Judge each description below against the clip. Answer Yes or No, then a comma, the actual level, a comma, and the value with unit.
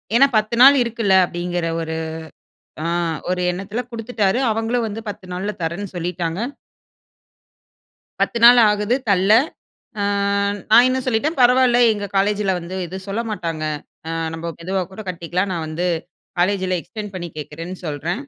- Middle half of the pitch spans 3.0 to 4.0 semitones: No, average, 4.4 semitones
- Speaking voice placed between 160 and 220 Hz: Yes, high, 195 Hz